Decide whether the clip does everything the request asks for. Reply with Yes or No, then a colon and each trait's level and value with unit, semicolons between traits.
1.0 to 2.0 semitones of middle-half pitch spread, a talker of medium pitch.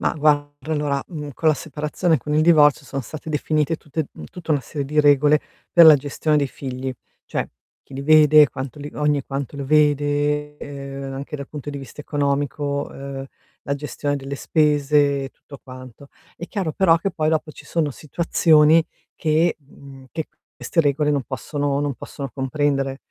Yes: narrow, 1.7 semitones; medium, 145 Hz